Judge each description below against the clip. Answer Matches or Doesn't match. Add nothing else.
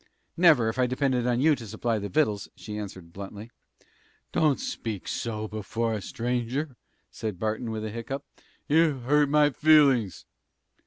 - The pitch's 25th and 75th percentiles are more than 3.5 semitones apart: Matches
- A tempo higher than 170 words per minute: Doesn't match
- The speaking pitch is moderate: Doesn't match